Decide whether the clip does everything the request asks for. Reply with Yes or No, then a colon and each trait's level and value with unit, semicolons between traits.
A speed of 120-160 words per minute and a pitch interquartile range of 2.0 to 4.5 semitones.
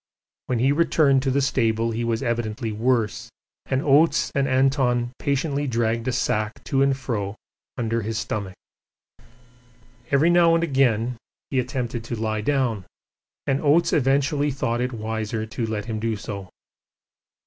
Yes: average, 150 wpm; average, 3.5 semitones